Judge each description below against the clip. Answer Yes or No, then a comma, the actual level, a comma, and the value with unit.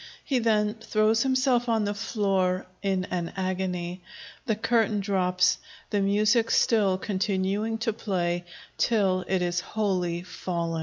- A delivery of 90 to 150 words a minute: Yes, slow, 135 wpm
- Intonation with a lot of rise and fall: No, average, 3.1 semitones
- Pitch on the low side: No, high, 195 Hz